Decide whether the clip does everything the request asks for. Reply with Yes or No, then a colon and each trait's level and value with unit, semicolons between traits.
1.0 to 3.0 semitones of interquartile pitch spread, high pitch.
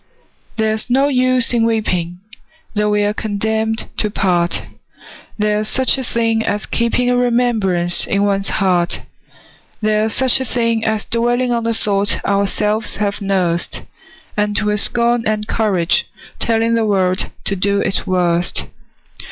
Yes: narrow, 2.6 semitones; high, 215 Hz